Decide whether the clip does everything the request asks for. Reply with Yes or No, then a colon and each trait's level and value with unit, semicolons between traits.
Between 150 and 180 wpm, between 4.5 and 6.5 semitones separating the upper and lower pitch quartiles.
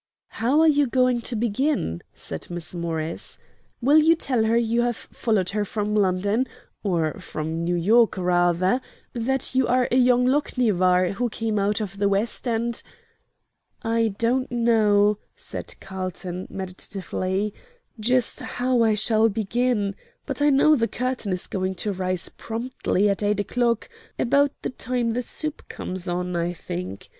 Yes: average, 155 wpm; average, 4.8 semitones